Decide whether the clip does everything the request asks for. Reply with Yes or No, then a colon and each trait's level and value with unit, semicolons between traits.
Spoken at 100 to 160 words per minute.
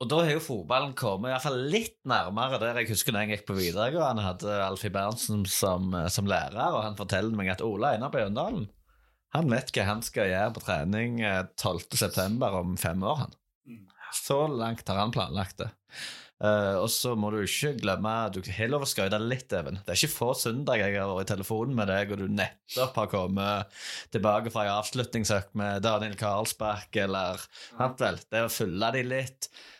No: fast, 205 wpm